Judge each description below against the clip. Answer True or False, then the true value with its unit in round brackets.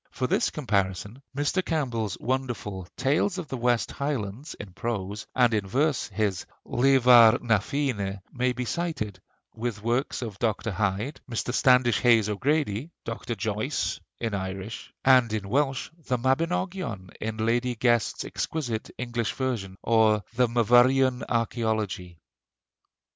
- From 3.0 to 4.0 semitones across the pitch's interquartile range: True (3.7 semitones)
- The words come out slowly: True (130 wpm)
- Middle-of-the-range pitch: False (120 Hz)